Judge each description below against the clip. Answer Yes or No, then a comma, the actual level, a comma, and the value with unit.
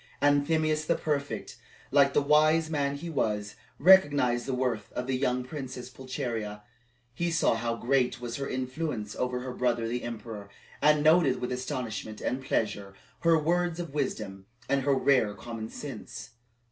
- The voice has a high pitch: No, low, 130 Hz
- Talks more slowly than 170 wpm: Yes, average, 160 wpm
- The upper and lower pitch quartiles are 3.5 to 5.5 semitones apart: Yes, average, 4.0 semitones